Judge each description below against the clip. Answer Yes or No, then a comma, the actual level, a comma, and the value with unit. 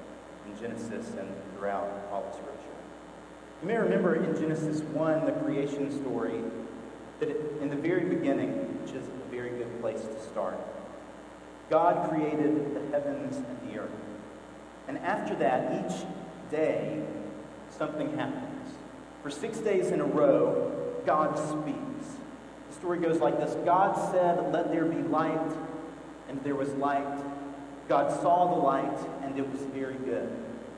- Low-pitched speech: No, medium, 155 Hz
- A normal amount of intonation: No, wide, 6.5 semitones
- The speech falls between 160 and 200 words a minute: No, average, 145 wpm